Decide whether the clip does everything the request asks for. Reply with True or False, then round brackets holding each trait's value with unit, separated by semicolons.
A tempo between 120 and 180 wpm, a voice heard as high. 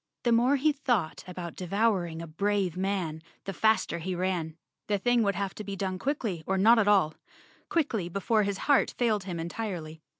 False (190 wpm; 195 Hz)